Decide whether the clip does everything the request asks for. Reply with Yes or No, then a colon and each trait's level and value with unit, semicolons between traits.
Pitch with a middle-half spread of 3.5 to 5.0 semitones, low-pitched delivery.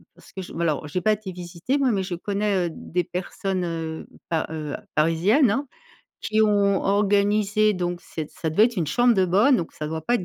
No: average, 4.0 semitones; high, 190 Hz